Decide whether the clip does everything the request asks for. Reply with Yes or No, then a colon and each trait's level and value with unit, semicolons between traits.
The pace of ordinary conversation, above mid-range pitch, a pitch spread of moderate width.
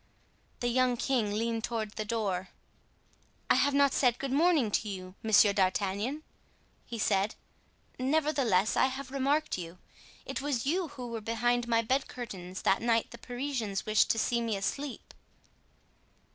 Yes: average, 155 wpm; high, 235 Hz; average, 4.3 semitones